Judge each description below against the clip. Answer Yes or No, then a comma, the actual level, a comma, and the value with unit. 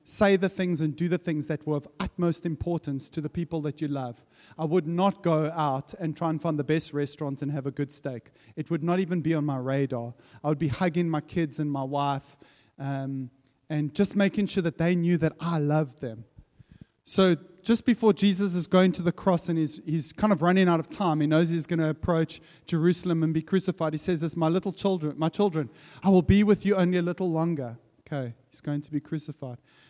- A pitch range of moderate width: Yes, average, 3.4 semitones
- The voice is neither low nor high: Yes, medium, 160 Hz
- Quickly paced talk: Yes, fast, 235 wpm